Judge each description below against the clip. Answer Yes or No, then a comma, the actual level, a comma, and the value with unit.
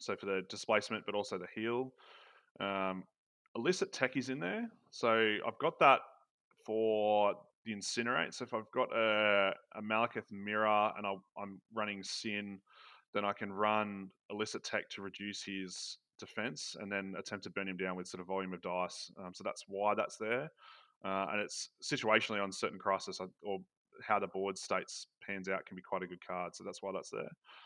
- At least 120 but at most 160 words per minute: No, average, 195 wpm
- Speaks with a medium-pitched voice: No, low, 100 Hz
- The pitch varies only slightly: Yes, narrow, 1.9 semitones